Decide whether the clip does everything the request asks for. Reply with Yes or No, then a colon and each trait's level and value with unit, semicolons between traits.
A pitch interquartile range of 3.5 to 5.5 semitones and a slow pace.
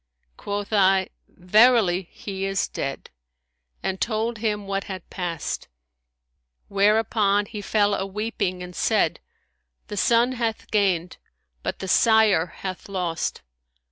No: narrow, 2.6 semitones; slow, 120 wpm